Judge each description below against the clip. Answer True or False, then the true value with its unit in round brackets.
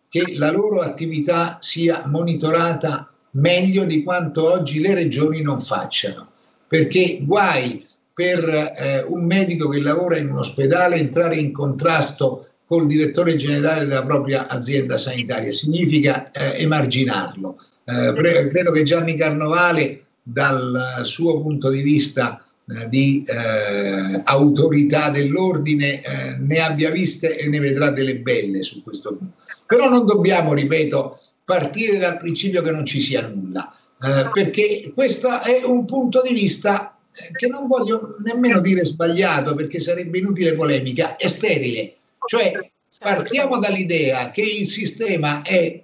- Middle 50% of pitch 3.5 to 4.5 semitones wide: True (4.1 semitones)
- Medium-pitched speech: True (160 Hz)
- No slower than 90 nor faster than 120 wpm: False (135 wpm)